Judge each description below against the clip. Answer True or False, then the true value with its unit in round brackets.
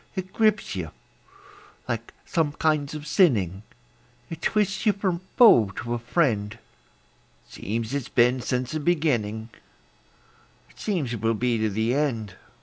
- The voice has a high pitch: False (130 Hz)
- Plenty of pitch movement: True (6.9 semitones)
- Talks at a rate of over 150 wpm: False (145 wpm)